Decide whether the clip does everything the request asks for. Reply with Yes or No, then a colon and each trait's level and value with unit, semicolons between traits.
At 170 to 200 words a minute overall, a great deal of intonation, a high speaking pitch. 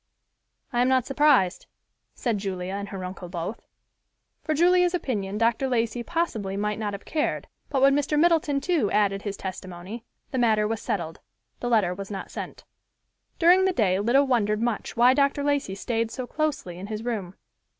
Yes: average, 175 wpm; wide, 5.9 semitones; high, 225 Hz